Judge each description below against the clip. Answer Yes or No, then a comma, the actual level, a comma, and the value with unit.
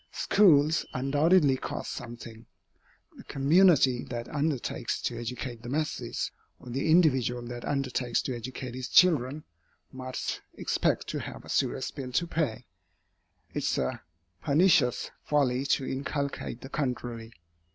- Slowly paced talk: Yes, slow, 130 wpm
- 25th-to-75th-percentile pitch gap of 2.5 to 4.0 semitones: Yes, average, 3.3 semitones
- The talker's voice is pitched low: Yes, low, 130 Hz